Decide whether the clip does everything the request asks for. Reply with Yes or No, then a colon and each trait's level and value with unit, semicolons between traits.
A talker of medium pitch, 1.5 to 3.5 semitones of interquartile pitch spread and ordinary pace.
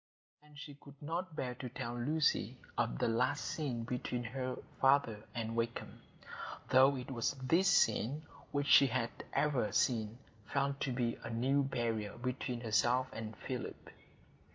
No: low, 125 Hz; average, 3.2 semitones; average, 155 wpm